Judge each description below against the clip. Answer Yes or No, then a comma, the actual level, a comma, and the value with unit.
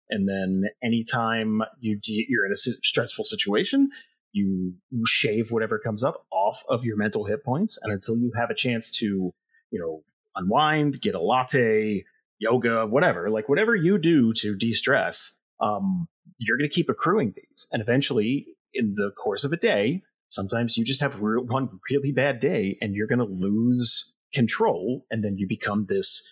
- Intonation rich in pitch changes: Yes, wide, 5.7 semitones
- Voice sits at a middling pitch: No, low, 115 Hz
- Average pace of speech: Yes, average, 180 wpm